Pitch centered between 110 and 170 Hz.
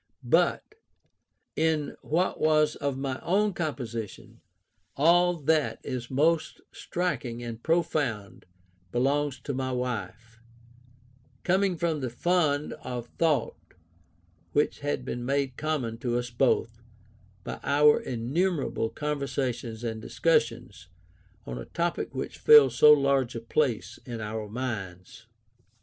Yes: low, 135 Hz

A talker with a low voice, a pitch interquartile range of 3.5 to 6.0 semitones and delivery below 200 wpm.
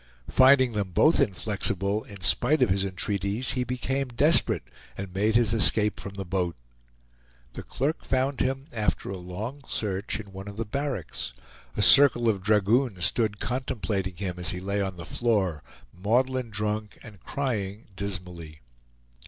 Yes: low, 105 Hz; average, 4.5 semitones; average, 155 wpm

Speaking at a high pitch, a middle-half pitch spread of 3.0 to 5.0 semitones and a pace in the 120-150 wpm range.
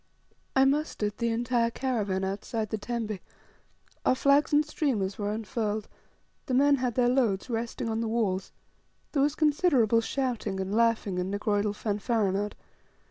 Yes: high, 230 Hz; average, 3.8 semitones; average, 145 wpm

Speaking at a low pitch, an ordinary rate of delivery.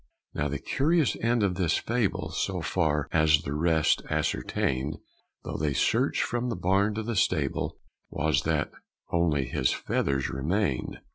Yes: very low, 80 Hz; average, 150 wpm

